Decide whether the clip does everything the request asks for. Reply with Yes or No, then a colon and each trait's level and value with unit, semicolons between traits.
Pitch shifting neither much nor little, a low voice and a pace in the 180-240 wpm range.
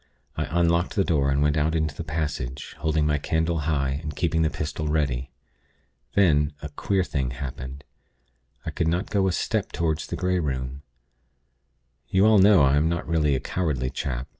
Yes: average, 3.2 semitones; very low, 75 Hz; average, 185 wpm